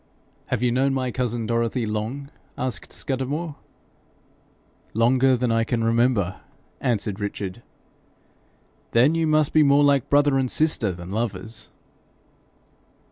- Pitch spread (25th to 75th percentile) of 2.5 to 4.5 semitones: Yes, average, 3.5 semitones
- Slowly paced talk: Yes, slow, 125 wpm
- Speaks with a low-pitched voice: Yes, low, 125 Hz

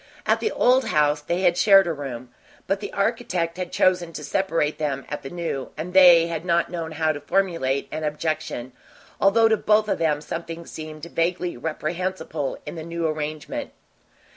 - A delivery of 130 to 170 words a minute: No, average, 180 wpm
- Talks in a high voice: No, medium, 165 Hz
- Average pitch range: Yes, average, 3.3 semitones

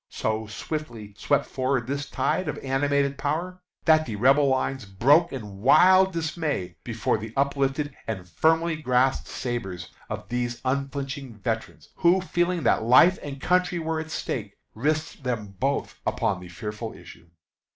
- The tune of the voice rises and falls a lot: Yes, wide, 5.7 semitones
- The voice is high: No, low, 135 Hz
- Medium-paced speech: Yes, average, 150 wpm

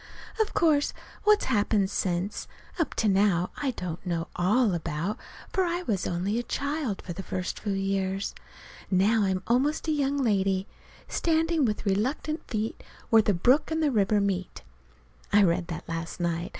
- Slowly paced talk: No, average, 165 wpm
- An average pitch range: No, wide, 6.4 semitones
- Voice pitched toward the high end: Yes, high, 205 Hz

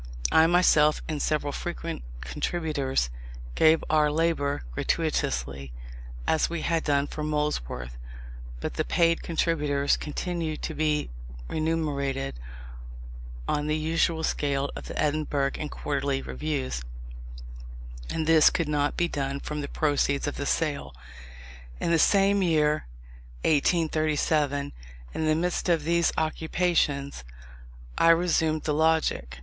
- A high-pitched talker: No, medium, 150 Hz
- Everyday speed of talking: No, slow, 125 wpm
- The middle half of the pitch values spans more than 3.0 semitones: No, narrow, 2.4 semitones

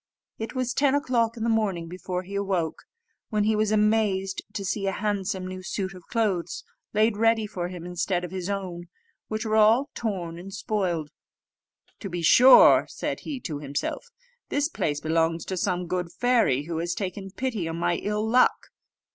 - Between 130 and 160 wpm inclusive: No, average, 180 wpm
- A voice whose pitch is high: Yes, high, 195 Hz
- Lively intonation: No, average, 3.9 semitones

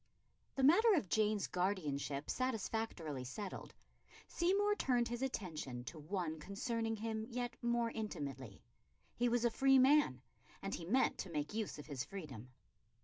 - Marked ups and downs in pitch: Yes, wide, 7.8 semitones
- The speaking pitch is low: No, high, 210 Hz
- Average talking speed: Yes, average, 145 wpm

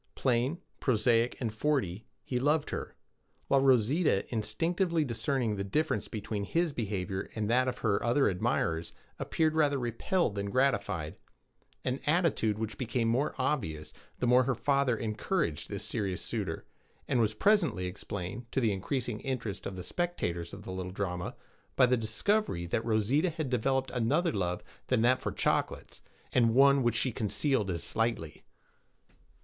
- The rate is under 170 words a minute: Yes, average, 155 wpm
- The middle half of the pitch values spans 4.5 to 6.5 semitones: Yes, average, 5.2 semitones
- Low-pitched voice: Yes, low, 120 Hz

